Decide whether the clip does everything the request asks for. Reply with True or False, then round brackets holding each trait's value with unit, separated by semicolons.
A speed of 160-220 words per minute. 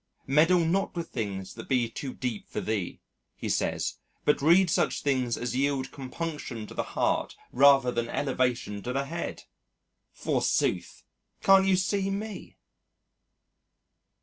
False (140 wpm)